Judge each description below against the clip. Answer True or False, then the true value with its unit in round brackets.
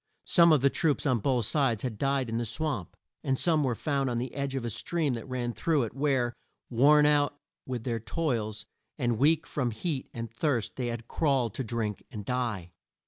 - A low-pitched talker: True (125 Hz)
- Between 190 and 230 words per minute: True (205 wpm)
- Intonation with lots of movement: False (3.7 semitones)